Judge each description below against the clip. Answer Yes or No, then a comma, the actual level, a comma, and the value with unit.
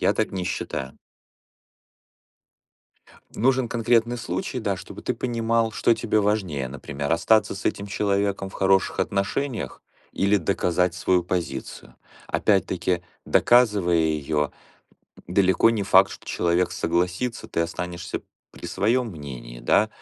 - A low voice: Yes, very low, 95 Hz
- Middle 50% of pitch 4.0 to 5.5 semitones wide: Yes, average, 4.4 semitones